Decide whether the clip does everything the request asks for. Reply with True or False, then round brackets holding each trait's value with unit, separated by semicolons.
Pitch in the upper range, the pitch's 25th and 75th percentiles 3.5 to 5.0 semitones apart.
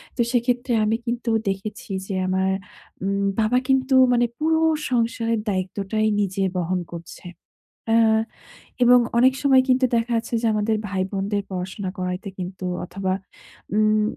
True (215 Hz; 4.0 semitones)